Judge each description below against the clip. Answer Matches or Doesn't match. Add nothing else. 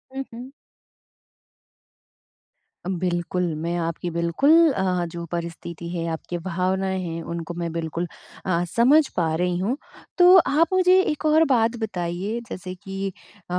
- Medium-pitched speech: Matches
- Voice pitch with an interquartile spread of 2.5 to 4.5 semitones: Doesn't match